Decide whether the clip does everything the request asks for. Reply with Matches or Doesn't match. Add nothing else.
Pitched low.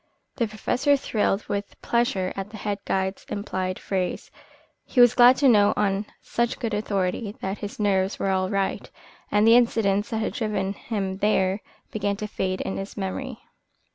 Doesn't match